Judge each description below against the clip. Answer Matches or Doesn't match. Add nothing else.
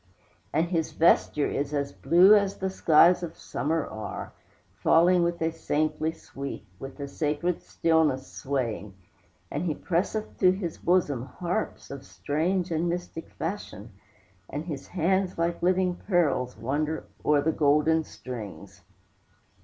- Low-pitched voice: Doesn't match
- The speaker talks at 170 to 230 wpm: Doesn't match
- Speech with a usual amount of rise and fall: Matches